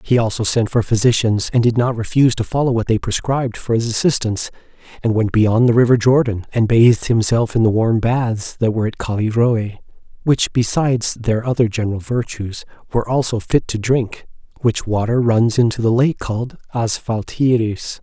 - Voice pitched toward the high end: No, low, 115 Hz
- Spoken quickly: No, average, 175 wpm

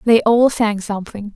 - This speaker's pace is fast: No, average, 175 wpm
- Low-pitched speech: No, high, 215 Hz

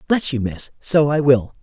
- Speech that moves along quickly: Yes, fast, 220 wpm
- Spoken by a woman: Yes, female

